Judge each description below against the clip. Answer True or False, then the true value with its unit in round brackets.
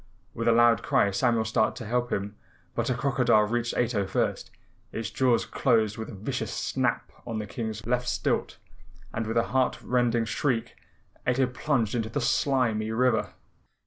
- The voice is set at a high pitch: False (115 Hz)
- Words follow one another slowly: False (170 wpm)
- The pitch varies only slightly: True (2.0 semitones)